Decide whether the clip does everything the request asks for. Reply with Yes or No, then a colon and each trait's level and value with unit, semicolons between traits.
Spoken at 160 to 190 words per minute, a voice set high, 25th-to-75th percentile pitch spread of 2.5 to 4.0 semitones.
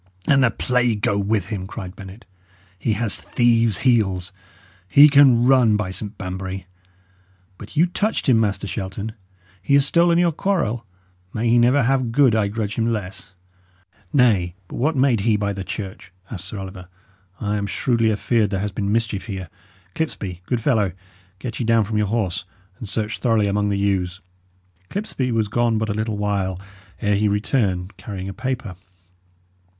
No: average, 175 wpm; low, 105 Hz; average, 3.4 semitones